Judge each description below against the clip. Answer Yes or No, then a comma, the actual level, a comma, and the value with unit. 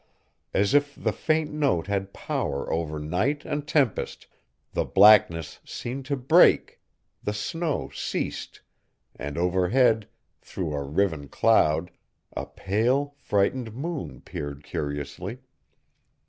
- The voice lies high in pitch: No, low, 100 Hz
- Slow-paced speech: Yes, slow, 115 wpm